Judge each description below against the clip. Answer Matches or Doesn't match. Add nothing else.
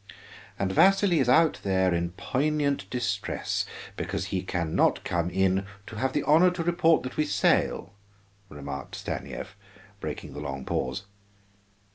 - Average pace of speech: Matches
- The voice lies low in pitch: Matches